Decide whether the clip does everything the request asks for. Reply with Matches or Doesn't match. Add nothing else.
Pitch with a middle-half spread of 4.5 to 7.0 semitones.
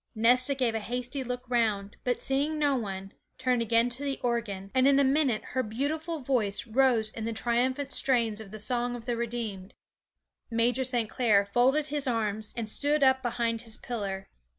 Doesn't match